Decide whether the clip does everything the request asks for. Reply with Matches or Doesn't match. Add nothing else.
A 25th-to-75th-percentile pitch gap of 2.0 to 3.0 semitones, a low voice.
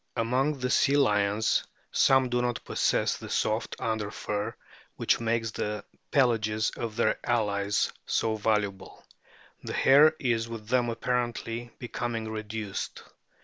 Matches